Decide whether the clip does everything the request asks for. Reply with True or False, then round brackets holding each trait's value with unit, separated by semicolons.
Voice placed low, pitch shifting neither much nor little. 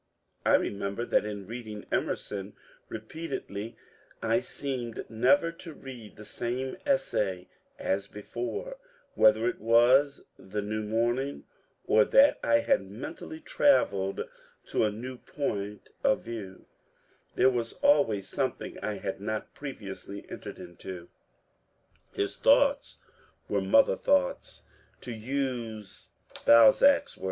True (115 Hz; 5.0 semitones)